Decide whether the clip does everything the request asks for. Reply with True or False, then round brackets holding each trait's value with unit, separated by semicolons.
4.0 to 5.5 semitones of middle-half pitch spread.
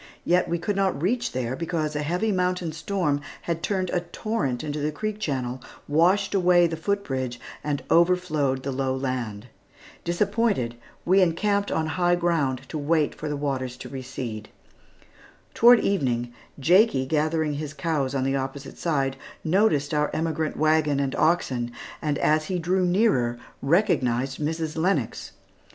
True (5.0 semitones)